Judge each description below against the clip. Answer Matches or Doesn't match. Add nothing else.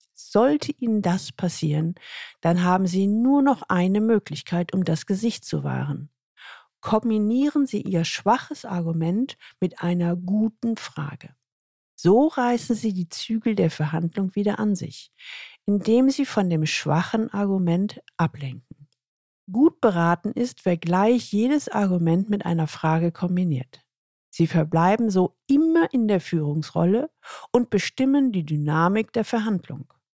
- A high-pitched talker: Matches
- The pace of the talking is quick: Doesn't match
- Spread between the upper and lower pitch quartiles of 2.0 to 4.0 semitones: Doesn't match